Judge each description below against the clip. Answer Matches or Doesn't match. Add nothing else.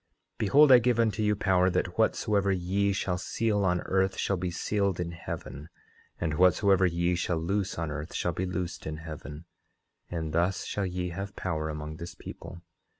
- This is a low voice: Matches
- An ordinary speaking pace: Matches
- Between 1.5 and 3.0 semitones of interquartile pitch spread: Matches